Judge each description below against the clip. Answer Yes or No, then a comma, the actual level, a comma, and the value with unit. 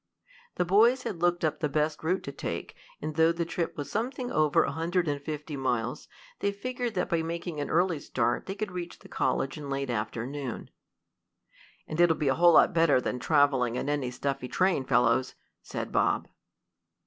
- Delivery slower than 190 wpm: No, average, 195 wpm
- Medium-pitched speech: Yes, medium, 155 Hz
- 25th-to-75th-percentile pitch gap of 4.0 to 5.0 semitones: Yes, average, 4.3 semitones